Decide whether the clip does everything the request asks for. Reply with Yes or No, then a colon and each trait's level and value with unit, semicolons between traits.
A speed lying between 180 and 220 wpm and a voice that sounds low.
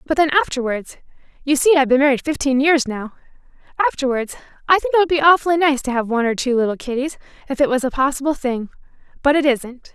No: average, 200 wpm; very high, 275 Hz